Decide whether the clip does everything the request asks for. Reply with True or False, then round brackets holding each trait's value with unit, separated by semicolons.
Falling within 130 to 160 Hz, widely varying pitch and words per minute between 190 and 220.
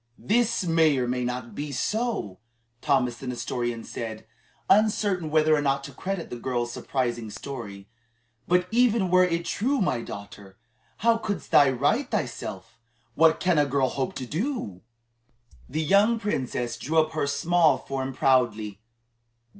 False (140 Hz; 6.8 semitones; 150 wpm)